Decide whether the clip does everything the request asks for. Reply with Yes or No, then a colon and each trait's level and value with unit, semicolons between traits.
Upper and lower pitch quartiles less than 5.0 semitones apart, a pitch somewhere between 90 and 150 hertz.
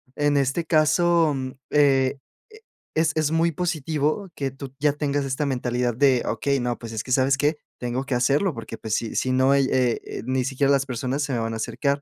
Yes: narrow, 2.5 semitones; medium, 140 Hz